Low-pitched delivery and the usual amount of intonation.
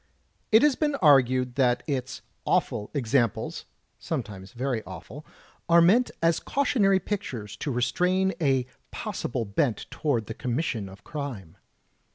No: low, 130 Hz; wide, 6.5 semitones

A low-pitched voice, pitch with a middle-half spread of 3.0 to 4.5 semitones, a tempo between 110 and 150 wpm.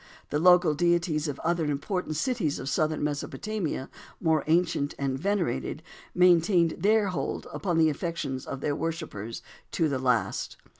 No: medium, 160 Hz; average, 3.5 semitones; average, 145 wpm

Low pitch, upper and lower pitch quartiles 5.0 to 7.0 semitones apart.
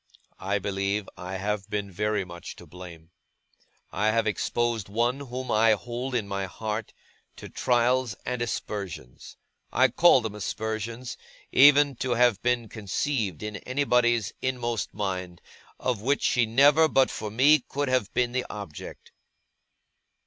No: low, 115 Hz; average, 3.9 semitones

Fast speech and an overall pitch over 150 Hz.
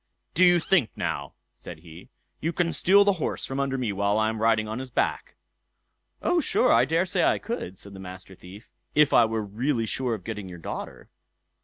No: fast, 210 wpm; low, 115 Hz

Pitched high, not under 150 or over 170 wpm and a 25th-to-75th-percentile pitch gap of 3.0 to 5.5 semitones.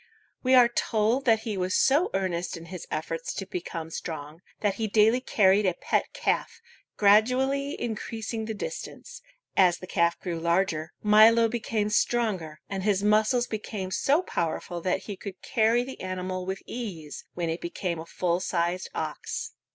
Yes: high, 195 Hz; average, 165 wpm; average, 4.3 semitones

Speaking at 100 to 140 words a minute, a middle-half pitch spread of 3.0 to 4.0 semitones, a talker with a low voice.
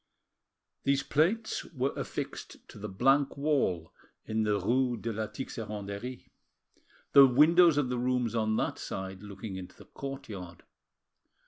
No: slow, 135 wpm; average, 5.1 semitones; low, 120 Hz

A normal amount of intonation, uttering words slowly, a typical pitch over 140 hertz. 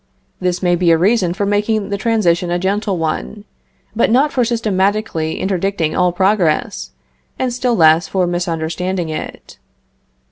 No: average, 3.7 semitones; average, 145 wpm; medium, 185 Hz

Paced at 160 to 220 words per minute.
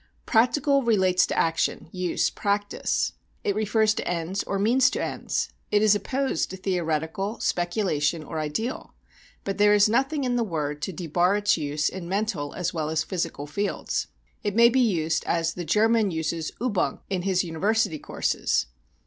Yes: average, 165 wpm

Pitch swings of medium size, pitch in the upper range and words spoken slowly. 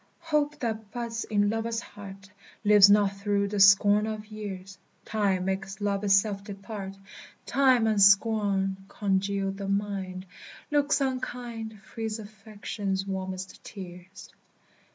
No: narrow, 2.1 semitones; high, 205 Hz; slow, 120 wpm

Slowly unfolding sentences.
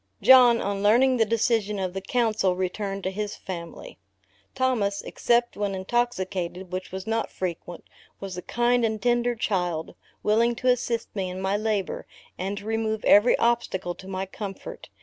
No: average, 165 wpm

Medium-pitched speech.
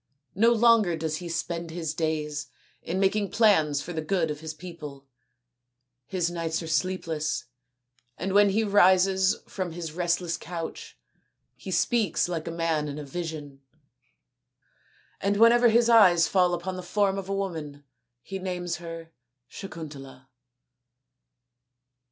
Yes: medium, 175 Hz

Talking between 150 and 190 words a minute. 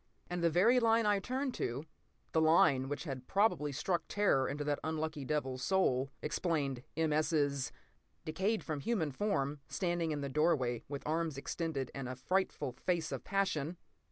Yes: average, 165 wpm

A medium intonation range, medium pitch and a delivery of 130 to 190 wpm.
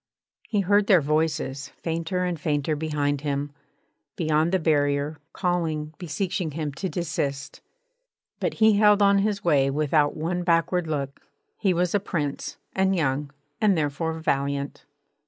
Yes: average, 3.8 semitones; medium, 160 Hz; average, 140 wpm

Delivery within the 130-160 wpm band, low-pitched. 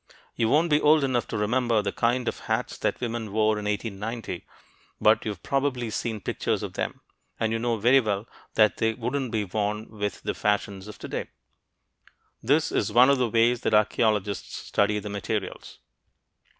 No: average, 175 wpm; low, 110 Hz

